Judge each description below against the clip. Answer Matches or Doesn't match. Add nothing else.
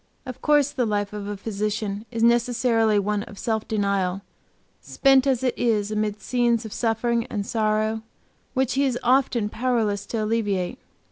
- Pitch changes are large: Doesn't match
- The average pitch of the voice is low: Doesn't match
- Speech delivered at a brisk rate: Doesn't match